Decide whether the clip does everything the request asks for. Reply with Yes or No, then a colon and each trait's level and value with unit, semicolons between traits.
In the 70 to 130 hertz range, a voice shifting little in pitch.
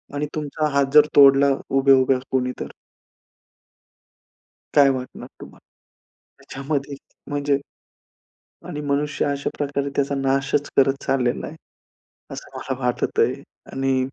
No: medium, 140 Hz; narrow, 1.2 semitones